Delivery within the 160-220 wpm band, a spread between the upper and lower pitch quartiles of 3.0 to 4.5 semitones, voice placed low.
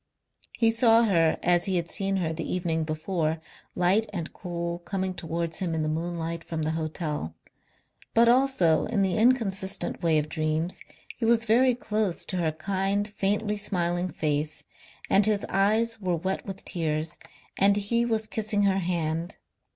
No: average, 165 wpm; average, 4.2 semitones; medium, 185 Hz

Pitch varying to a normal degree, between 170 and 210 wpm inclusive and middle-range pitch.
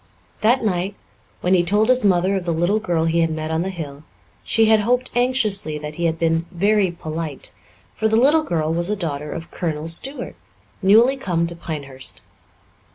Yes: average, 4.9 semitones; average, 190 wpm; medium, 175 Hz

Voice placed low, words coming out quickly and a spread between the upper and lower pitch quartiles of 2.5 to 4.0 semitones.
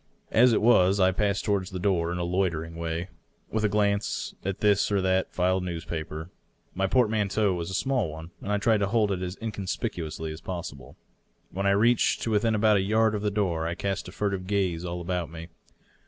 Yes: very low, 95 Hz; fast, 215 wpm; average, 3.2 semitones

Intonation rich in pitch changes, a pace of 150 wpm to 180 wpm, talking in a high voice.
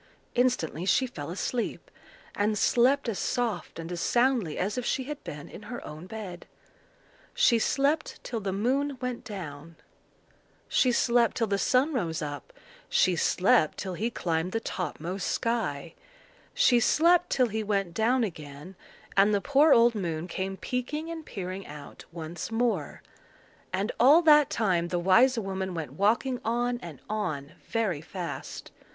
Yes: wide, 6.0 semitones; average, 155 wpm; high, 210 Hz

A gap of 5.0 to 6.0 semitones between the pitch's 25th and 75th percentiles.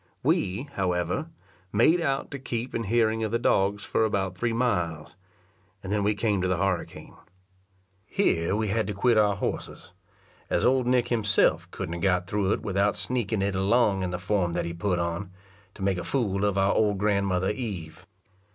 No: average, 3.4 semitones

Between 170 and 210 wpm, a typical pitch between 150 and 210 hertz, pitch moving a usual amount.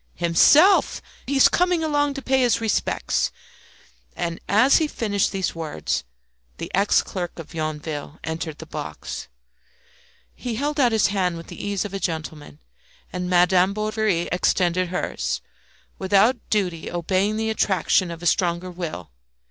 No: average, 145 wpm; high, 190 Hz; average, 4.6 semitones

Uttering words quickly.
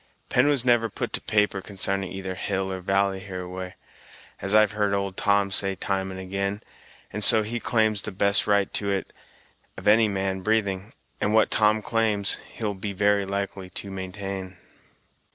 No: average, 170 wpm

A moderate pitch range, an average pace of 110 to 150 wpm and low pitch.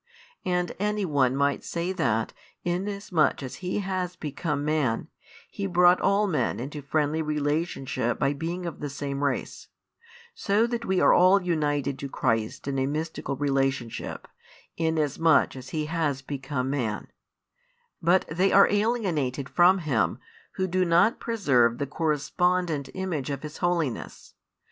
No: average, 4.7 semitones; average, 145 wpm; medium, 155 Hz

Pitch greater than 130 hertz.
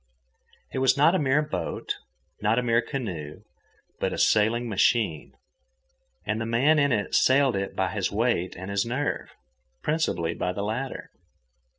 No: low, 115 Hz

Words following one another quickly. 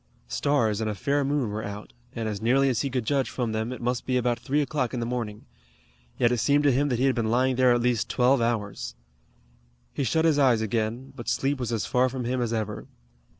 Yes: fast, 240 wpm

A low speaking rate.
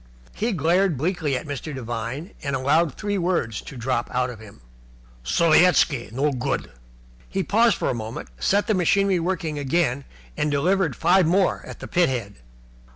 No: average, 160 wpm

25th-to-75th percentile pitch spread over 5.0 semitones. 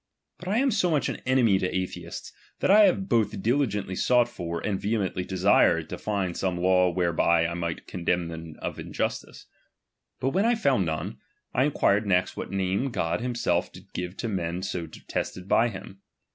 Yes: wide, 5.6 semitones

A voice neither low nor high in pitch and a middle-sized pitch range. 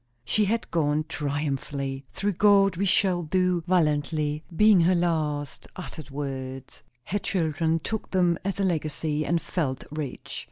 Yes: medium, 160 Hz; average, 3.9 semitones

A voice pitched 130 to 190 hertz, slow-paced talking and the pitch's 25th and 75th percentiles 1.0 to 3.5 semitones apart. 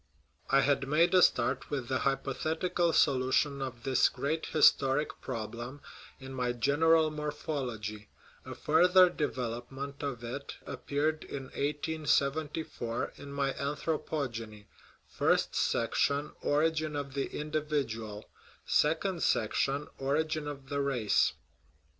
Yes: medium, 140 Hz; slow, 115 wpm; average, 2.9 semitones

